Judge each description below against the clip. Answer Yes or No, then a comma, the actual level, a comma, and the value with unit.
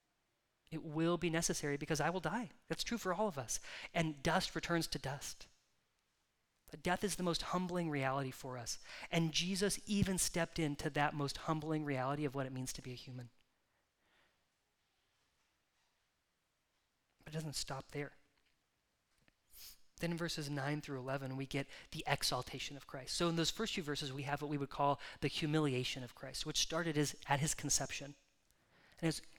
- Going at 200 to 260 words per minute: No, average, 175 wpm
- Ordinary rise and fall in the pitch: Yes, average, 3.3 semitones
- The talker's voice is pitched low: No, medium, 150 Hz